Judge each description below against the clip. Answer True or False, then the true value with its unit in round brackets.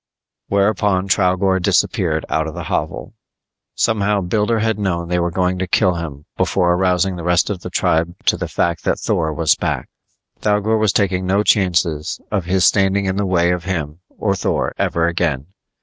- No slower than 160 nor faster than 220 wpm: True (180 wpm)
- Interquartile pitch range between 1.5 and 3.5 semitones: True (2.6 semitones)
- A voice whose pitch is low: True (90 Hz)